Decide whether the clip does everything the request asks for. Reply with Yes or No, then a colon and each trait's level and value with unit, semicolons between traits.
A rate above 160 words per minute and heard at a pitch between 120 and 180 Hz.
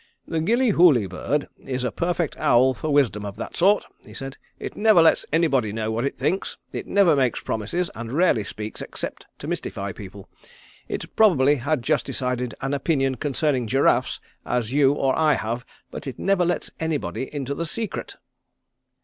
Yes: average, 175 wpm; low, 135 Hz